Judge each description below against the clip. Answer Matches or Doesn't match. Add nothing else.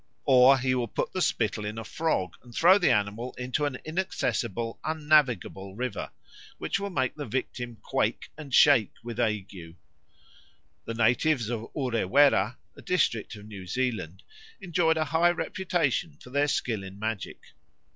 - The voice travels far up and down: Matches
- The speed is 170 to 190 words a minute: Doesn't match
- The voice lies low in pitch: Matches